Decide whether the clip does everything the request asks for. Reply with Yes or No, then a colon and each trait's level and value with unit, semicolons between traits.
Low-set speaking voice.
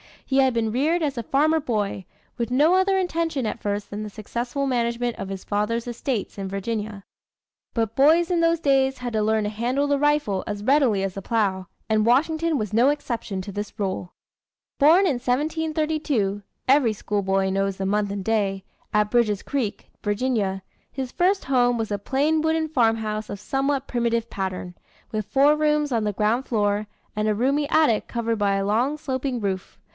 No: high, 235 Hz